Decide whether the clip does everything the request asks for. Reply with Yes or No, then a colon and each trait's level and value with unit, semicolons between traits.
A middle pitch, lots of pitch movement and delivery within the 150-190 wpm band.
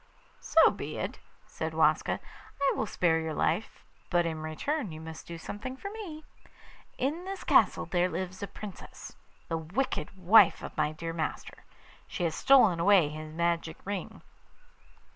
Yes: medium, 180 Hz; wide, 5.8 semitones; average, 160 wpm